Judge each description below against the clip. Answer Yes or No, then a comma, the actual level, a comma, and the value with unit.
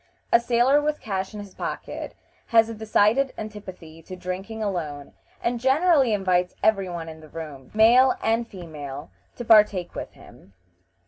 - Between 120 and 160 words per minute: Yes, average, 155 wpm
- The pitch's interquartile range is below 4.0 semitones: No, average, 4.8 semitones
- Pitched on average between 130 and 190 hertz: No, high, 205 Hz